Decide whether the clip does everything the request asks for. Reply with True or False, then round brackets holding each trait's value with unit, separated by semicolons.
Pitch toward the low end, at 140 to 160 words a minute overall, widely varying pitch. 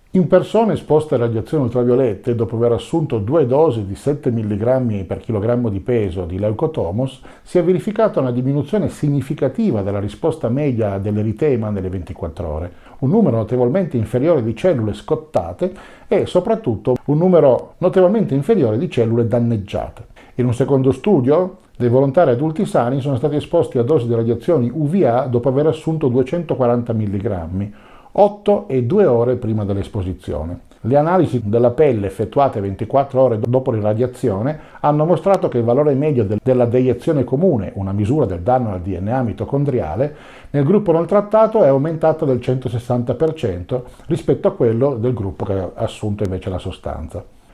True (125 Hz; 150 wpm; 6.0 semitones)